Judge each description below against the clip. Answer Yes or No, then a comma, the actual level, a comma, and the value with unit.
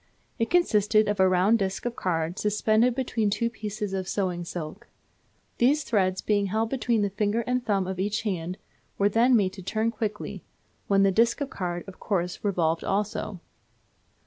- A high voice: Yes, high, 205 Hz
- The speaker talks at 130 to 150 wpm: No, average, 175 wpm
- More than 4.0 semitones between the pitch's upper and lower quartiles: No, average, 3.2 semitones